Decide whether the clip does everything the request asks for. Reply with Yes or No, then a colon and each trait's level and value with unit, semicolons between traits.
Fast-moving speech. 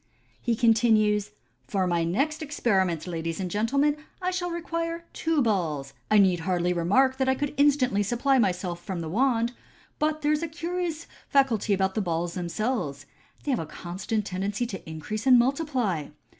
No: average, 175 wpm